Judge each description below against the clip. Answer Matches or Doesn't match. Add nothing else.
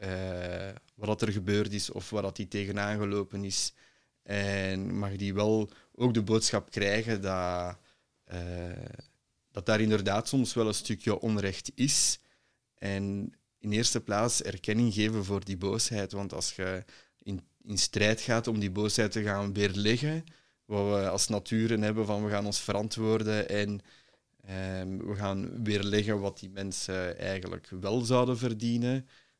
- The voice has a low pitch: Matches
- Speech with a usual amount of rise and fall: Doesn't match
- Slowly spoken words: Doesn't match